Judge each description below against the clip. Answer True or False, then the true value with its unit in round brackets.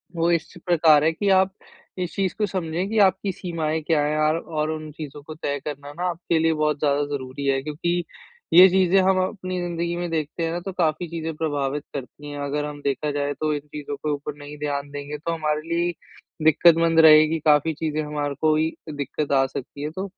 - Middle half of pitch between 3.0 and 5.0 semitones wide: False (2.6 semitones)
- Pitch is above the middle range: False (155 Hz)